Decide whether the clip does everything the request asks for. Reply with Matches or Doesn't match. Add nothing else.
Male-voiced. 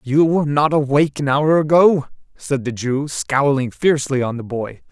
Matches